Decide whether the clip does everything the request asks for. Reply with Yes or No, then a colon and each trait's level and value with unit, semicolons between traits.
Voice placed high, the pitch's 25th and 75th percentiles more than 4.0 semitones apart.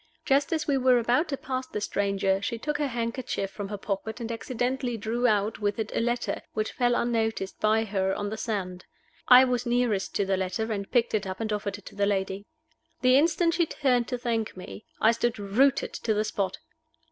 No: high, 225 Hz; average, 3.6 semitones